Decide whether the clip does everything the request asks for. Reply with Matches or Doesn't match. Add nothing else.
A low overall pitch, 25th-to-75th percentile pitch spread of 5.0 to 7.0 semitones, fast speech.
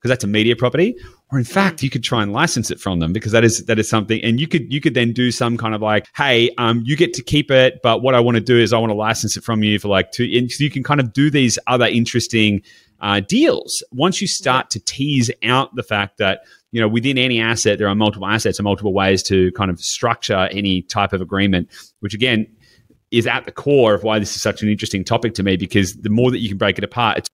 Doesn't match